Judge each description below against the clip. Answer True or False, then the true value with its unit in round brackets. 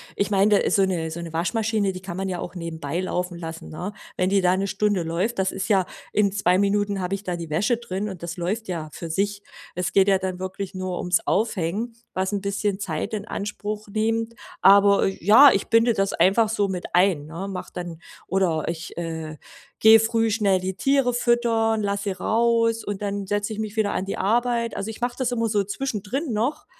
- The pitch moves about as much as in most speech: True (3.2 semitones)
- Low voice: False (200 Hz)